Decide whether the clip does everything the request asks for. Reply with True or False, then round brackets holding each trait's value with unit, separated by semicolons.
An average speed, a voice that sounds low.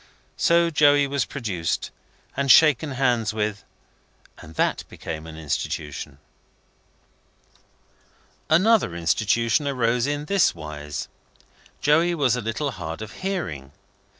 False (110 wpm; 120 Hz)